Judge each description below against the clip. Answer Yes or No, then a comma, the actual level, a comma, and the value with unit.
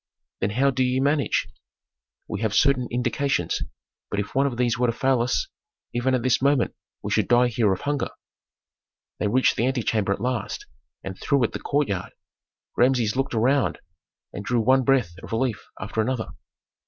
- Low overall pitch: Yes, low, 125 Hz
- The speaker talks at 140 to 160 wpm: No, average, 180 wpm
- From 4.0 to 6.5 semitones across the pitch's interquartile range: No, average, 3.1 semitones